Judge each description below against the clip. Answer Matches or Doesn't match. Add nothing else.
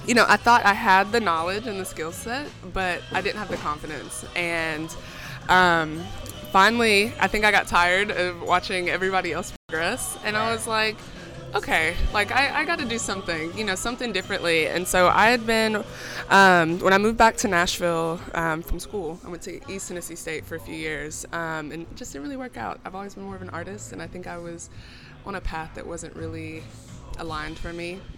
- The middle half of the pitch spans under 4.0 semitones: Doesn't match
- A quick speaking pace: Matches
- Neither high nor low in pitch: Matches